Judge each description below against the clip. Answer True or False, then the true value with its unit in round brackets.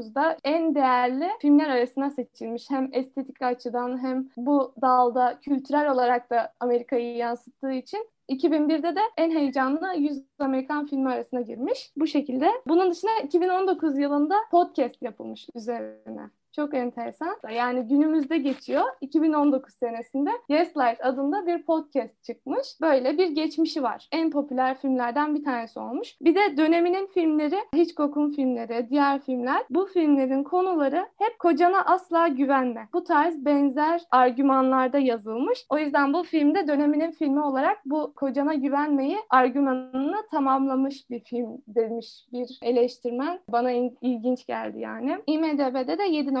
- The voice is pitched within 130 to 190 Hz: False (280 Hz)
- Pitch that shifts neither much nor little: True (4.0 semitones)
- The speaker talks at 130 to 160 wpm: True (135 wpm)